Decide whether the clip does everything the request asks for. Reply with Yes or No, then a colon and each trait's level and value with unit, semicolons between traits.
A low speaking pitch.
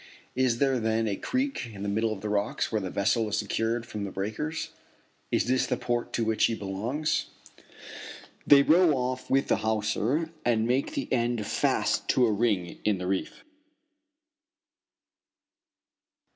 Yes: low, 115 Hz